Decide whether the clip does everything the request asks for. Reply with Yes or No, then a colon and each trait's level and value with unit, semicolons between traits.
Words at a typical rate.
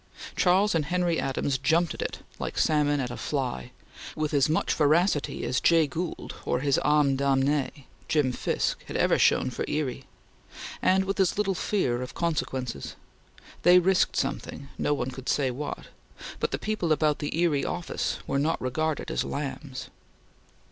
Yes: average, 165 wpm